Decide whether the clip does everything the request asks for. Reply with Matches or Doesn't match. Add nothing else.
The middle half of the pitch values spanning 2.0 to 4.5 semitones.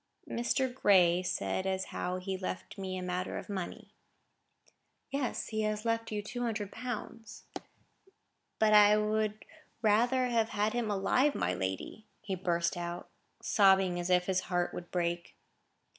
Matches